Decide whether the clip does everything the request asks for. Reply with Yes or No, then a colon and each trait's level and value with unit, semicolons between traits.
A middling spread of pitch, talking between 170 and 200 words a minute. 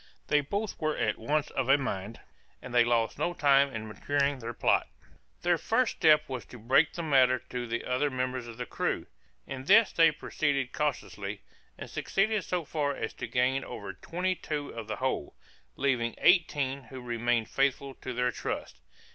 Yes: average, 3.8 semitones; average, 180 wpm